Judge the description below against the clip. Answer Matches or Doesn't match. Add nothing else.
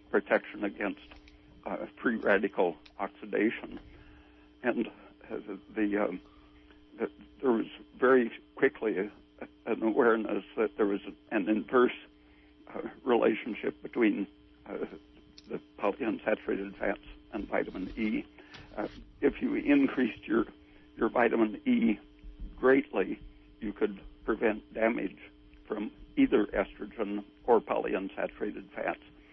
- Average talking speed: Doesn't match